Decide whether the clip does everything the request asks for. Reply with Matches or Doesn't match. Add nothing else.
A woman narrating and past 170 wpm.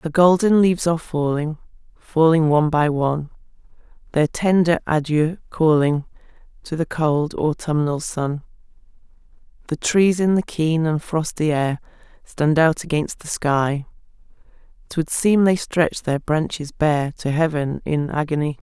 Doesn't match